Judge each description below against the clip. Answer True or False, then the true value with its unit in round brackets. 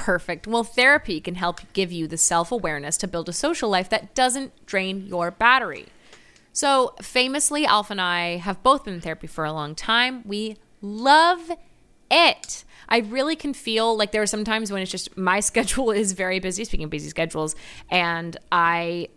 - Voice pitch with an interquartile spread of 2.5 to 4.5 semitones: False (5.3 semitones)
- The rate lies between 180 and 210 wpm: True (190 wpm)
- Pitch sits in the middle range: False (200 Hz)